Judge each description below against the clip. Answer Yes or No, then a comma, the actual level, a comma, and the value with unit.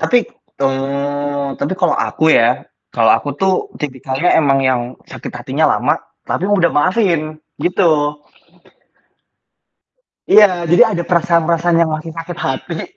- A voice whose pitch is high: No, medium, 160 Hz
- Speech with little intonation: No, average, 3.8 semitones